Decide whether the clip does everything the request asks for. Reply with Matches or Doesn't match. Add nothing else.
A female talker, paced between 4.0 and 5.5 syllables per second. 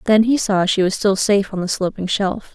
Matches